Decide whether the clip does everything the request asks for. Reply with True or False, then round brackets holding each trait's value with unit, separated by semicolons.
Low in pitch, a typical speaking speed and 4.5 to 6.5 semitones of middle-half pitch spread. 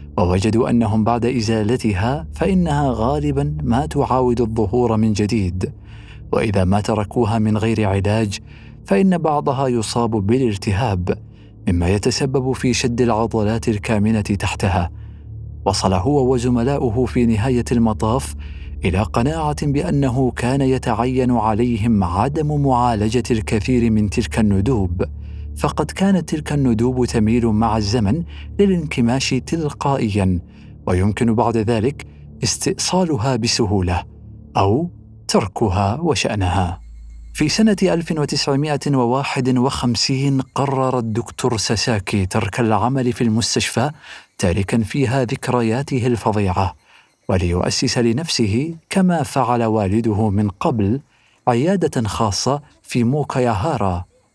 False (115 Hz; 95 wpm; 3.9 semitones)